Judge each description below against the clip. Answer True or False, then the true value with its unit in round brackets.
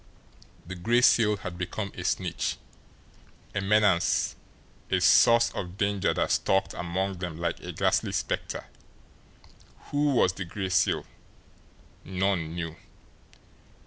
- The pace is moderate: False (120 wpm)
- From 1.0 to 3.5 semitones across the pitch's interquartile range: True (2.7 semitones)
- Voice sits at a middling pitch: False (95 Hz)